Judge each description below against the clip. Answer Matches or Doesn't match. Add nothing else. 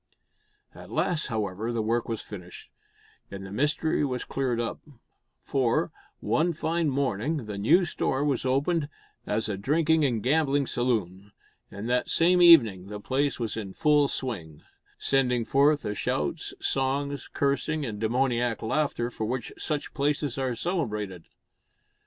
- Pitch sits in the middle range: Doesn't match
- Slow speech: Doesn't match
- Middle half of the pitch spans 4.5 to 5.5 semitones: Matches